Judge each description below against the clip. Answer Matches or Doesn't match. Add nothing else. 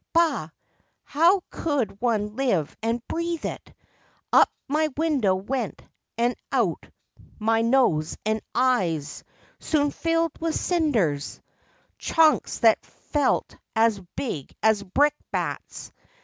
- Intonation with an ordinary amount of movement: Doesn't match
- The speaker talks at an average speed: Doesn't match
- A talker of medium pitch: Doesn't match